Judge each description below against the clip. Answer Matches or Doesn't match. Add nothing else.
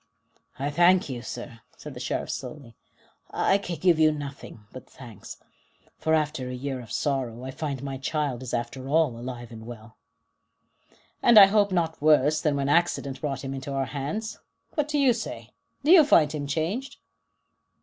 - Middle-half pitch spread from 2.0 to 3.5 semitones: Doesn't match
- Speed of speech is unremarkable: Matches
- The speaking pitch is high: Doesn't match